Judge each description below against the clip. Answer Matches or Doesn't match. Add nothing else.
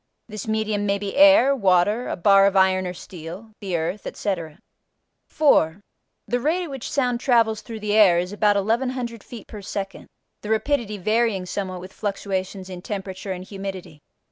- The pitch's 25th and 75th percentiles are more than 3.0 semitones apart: Matches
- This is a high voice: Matches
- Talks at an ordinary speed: Matches